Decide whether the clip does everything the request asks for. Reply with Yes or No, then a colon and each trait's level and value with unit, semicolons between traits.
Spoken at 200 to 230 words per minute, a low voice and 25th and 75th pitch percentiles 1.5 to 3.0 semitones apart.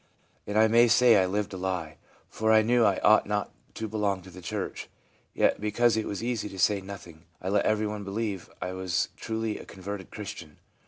Yes: fast, 205 wpm; low, 105 Hz; average, 2.7 semitones